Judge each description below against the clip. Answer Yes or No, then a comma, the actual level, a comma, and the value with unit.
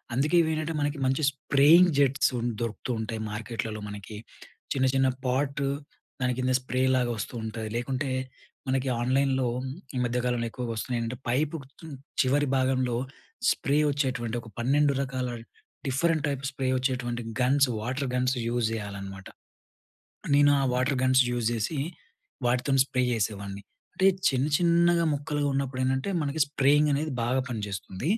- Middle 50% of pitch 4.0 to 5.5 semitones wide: No, average, 2.9 semitones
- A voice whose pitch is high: No, low, 130 Hz